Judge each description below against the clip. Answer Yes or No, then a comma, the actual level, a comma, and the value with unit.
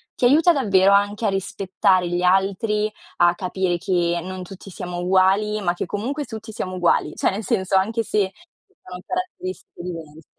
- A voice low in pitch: No, high, 195 Hz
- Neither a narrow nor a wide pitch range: Yes, average, 3.3 semitones